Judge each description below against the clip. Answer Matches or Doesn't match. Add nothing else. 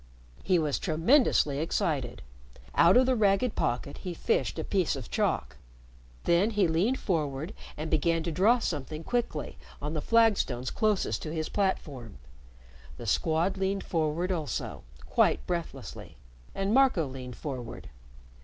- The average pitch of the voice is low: Doesn't match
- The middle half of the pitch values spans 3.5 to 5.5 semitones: Matches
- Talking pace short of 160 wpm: Matches